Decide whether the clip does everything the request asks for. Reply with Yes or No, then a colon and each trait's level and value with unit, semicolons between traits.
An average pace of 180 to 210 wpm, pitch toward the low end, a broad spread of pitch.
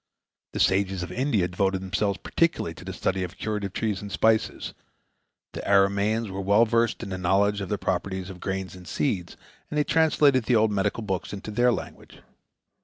No: average, 185 wpm; low, 100 Hz; average, 2.8 semitones